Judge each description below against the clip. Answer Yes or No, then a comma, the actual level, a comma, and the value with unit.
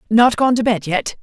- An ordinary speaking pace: No, fast, 245 wpm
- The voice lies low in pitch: No, high, 225 Hz